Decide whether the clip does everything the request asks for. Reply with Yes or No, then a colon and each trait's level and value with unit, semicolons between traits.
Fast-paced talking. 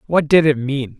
Yes: fast, 240 wpm